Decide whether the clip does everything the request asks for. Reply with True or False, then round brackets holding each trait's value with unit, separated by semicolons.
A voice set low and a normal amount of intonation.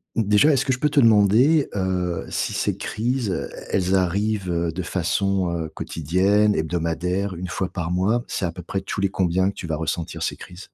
True (95 Hz; 3.2 semitones)